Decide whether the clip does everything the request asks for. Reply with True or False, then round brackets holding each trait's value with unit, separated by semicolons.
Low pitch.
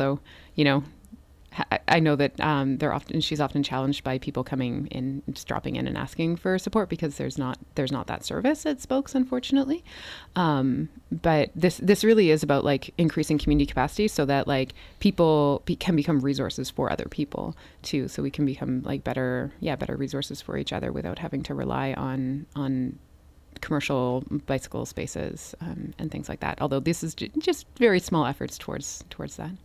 False (145 Hz)